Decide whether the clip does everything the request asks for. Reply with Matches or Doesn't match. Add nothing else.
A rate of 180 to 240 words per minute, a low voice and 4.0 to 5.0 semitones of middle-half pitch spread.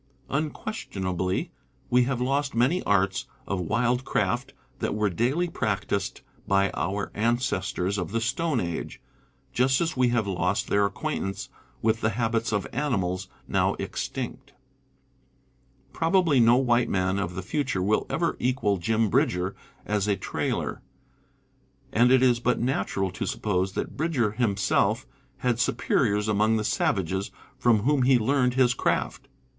Doesn't match